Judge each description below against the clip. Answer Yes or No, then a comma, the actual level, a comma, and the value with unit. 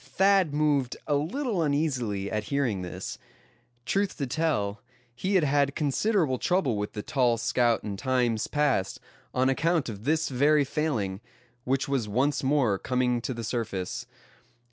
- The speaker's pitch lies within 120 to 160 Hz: Yes, low, 135 Hz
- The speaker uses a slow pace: No, average, 150 wpm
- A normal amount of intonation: Yes, average, 4.9 semitones